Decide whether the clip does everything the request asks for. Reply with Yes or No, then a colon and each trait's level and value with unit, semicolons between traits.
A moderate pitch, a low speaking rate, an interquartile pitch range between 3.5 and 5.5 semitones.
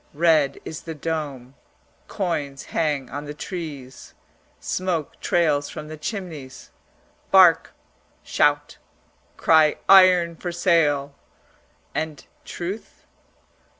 No: medium, 160 Hz; slow, 95 wpm; average, 3.1 semitones